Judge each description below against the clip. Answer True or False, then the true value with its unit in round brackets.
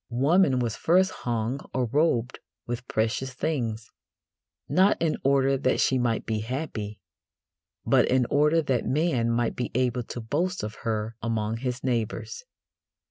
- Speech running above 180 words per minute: False (145 wpm)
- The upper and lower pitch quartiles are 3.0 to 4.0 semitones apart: True (3.6 semitones)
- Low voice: True (125 Hz)